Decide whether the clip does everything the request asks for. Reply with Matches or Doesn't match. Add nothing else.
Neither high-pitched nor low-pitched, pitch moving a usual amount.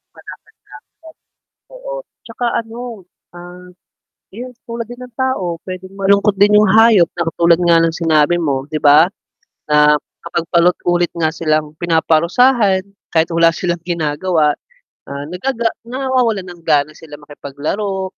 Matches